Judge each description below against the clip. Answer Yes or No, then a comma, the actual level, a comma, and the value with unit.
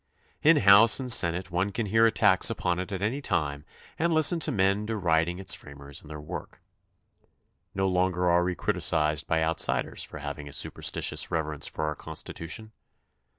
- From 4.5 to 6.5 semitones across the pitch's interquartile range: Yes, average, 5.2 semitones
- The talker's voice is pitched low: Yes, very low, 90 Hz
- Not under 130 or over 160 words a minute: No, average, 175 wpm